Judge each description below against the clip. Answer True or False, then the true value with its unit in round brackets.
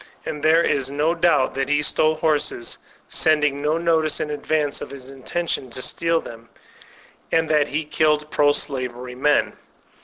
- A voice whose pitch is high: False (150 Hz)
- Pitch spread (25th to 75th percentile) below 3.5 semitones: True (2.5 semitones)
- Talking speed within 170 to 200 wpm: False (160 wpm)